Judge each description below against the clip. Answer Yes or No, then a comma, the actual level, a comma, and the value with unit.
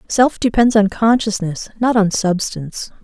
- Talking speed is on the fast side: No, average, 140 wpm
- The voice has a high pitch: Yes, high, 210 Hz